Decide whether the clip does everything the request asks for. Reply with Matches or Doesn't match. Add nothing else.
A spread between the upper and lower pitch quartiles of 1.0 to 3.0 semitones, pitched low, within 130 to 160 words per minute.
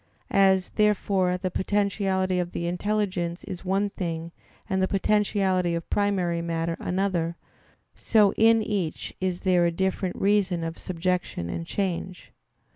Doesn't match